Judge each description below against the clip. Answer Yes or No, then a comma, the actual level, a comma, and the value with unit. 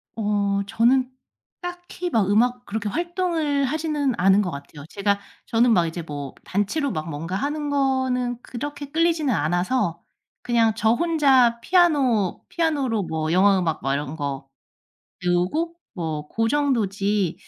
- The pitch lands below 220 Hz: No, high, 225 Hz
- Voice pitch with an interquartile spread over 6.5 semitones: Yes, wide, 7.9 semitones